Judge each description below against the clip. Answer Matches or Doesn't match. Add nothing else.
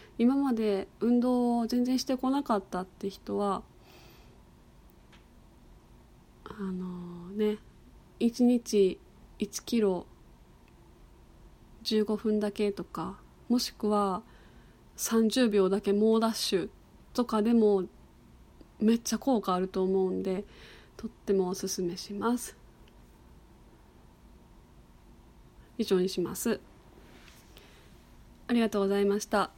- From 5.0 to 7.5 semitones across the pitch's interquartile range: Doesn't match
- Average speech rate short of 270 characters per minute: Matches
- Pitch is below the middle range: Doesn't match